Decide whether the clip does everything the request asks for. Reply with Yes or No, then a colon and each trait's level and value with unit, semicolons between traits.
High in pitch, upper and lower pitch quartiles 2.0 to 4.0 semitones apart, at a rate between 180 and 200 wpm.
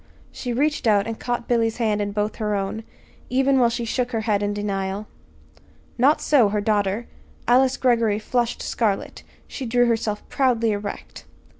No: high, 225 Hz; average, 2.9 semitones; average, 165 wpm